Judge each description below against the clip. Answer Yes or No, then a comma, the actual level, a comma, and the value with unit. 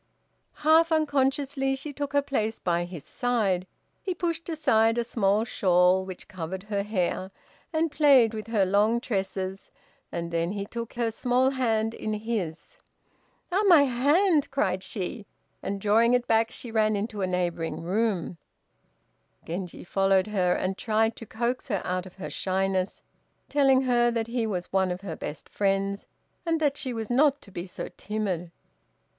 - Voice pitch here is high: Yes, high, 220 Hz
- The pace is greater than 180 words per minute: No, average, 165 wpm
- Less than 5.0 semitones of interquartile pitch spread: No, average, 5.3 semitones